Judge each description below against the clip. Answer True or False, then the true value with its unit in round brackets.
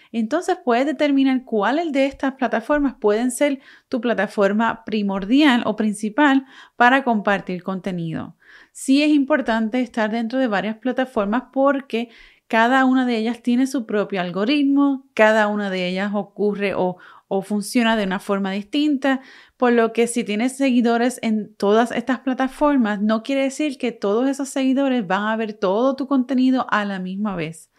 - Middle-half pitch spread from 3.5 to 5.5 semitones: True (4.4 semitones)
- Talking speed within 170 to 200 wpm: False (160 wpm)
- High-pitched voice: True (235 Hz)